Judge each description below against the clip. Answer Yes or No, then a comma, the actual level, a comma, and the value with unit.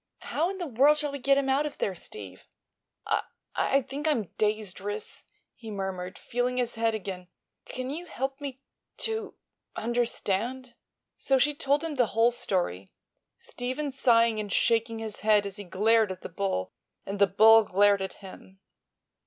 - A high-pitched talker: Yes, high, 230 Hz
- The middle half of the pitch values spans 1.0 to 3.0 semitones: No, average, 5.2 semitones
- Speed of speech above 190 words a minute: No, average, 165 wpm